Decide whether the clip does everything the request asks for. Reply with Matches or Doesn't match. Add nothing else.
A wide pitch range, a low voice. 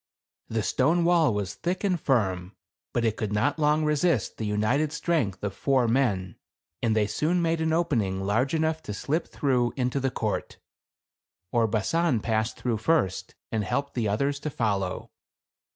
Matches